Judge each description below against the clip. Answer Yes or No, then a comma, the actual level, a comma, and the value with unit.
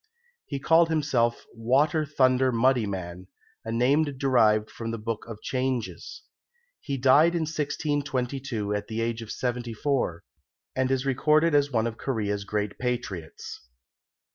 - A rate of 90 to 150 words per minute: Yes, average, 140 wpm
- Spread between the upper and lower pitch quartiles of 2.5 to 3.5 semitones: No, average, 4.0 semitones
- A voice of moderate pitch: No, low, 125 Hz